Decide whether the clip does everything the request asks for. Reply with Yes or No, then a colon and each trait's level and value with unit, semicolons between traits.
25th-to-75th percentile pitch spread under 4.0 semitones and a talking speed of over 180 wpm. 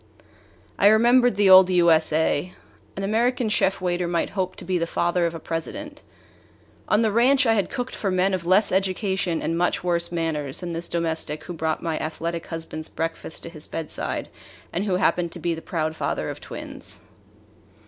Yes: average, 3.1 semitones; average, 190 wpm